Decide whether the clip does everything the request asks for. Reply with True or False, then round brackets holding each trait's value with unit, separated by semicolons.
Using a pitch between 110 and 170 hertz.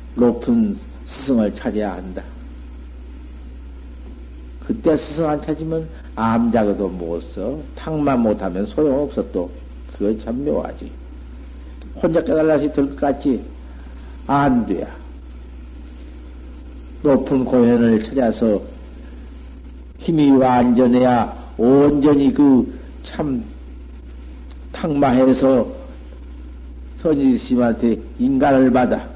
False (70 Hz)